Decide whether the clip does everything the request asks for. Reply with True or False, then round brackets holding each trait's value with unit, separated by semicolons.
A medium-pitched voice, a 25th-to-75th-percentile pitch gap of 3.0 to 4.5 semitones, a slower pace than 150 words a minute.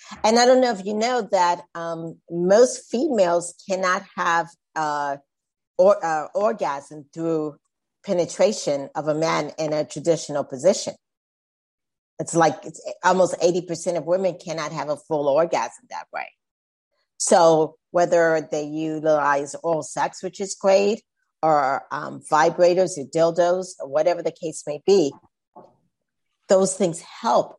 True (165 Hz; 3.3 semitones; 135 wpm)